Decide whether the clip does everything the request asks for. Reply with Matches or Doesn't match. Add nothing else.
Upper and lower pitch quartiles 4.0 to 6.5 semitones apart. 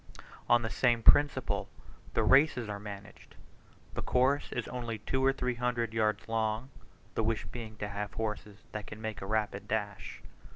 Doesn't match